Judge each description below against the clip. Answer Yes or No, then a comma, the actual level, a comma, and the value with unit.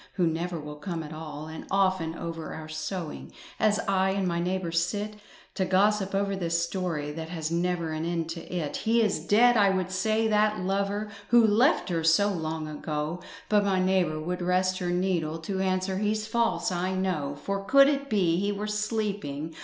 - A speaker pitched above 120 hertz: Yes, medium, 185 Hz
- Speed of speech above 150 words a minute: Yes, average, 190 wpm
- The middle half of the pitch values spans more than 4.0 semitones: No, average, 3.7 semitones